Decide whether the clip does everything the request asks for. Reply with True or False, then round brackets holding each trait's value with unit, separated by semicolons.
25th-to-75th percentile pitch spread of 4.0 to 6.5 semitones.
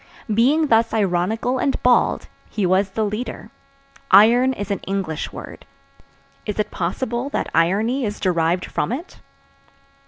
True (4.5 semitones)